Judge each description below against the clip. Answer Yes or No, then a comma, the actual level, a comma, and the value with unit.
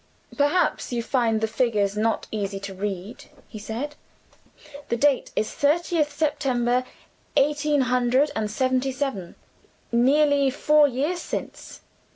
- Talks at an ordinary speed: No, slow, 125 wpm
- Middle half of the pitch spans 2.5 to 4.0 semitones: No, average, 4.7 semitones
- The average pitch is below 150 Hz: No, very high, 255 Hz